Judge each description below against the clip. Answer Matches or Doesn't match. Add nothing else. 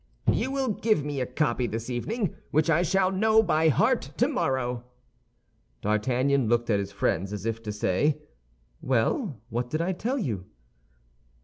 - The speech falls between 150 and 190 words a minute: Matches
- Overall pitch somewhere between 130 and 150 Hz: Matches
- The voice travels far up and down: Matches